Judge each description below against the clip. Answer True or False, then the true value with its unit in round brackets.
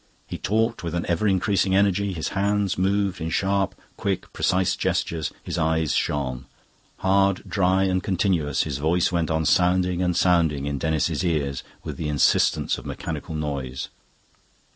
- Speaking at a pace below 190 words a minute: True (160 wpm)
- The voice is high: False (90 Hz)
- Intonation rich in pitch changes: False (3.6 semitones)